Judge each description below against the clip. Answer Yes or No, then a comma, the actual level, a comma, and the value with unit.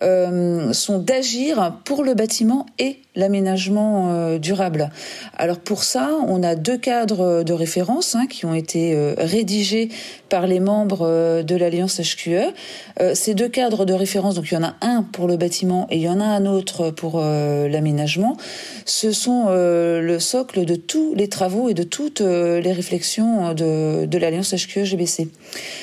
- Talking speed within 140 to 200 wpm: Yes, average, 175 wpm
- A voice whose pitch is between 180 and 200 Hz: Yes, medium, 185 Hz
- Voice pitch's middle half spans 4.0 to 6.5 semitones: Yes, average, 4.6 semitones